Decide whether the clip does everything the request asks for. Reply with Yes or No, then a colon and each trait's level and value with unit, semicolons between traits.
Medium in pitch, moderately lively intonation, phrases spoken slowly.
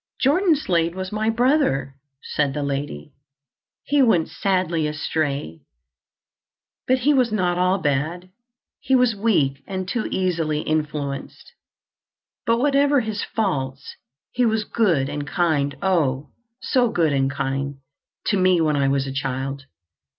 No: medium, 165 Hz; wide, 7.6 semitones; slow, 130 wpm